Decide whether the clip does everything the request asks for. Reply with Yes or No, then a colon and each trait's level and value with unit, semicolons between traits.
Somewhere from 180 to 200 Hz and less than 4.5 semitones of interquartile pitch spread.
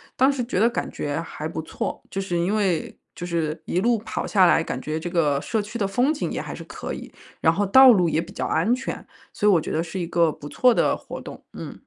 No: medium, 185 Hz; average, 5.3 semitones